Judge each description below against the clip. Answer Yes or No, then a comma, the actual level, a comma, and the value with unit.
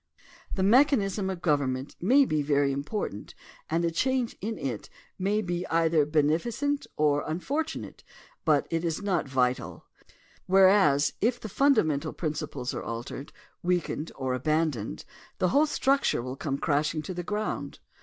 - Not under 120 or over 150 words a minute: Yes, average, 145 wpm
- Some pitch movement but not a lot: No, wide, 6.2 semitones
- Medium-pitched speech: Yes, medium, 165 Hz